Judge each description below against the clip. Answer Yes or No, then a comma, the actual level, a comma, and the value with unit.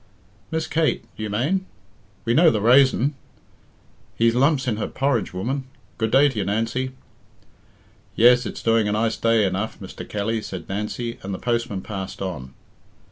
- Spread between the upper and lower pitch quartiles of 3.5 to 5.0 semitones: Yes, average, 4.0 semitones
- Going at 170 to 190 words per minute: No, average, 160 wpm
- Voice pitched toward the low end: Yes, low, 115 Hz